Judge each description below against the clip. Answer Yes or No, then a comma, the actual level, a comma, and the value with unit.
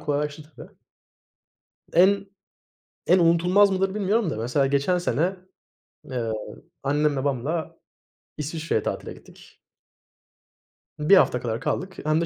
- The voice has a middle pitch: Yes, medium, 155 Hz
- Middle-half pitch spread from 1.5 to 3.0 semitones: No, average, 4.8 semitones